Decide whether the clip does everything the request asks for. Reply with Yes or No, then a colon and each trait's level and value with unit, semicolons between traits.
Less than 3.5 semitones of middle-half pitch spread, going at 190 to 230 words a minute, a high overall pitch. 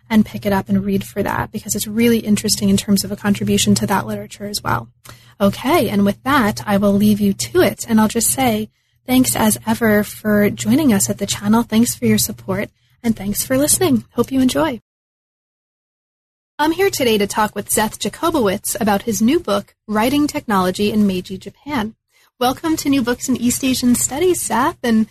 No: average, 3.8 semitones; average, 200 wpm; high, 215 Hz